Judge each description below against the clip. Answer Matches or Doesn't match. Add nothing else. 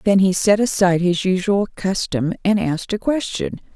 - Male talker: Doesn't match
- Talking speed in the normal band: Matches